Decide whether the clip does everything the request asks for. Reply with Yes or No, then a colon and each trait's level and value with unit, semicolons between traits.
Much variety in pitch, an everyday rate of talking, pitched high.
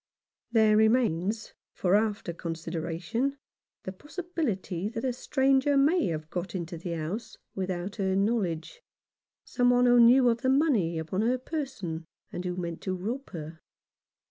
Yes: wide, 6.3 semitones; average, 150 wpm; high, 205 Hz